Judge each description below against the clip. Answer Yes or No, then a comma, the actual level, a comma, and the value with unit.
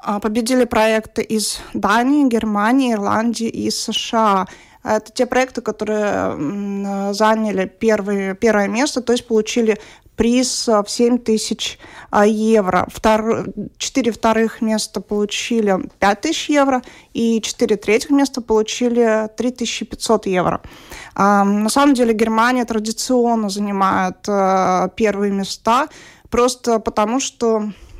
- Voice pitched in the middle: No, high, 220 Hz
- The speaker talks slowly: Yes, slow, 105 wpm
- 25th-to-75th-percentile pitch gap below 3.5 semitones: Yes, narrow, 2.5 semitones